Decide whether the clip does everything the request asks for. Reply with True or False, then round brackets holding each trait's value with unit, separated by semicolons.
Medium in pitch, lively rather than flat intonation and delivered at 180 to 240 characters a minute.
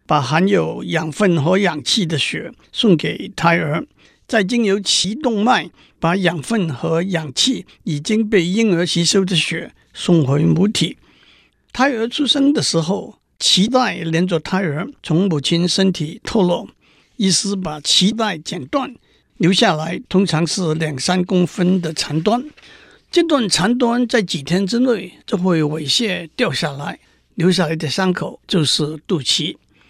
False (180 Hz; 4.5 semitones; 210 characters per minute)